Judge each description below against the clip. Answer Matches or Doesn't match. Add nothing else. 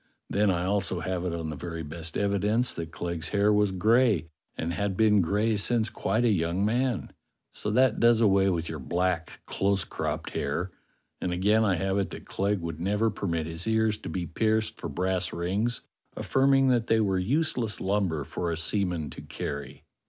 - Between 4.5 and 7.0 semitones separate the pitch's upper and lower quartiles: Doesn't match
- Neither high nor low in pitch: Doesn't match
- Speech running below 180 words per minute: Doesn't match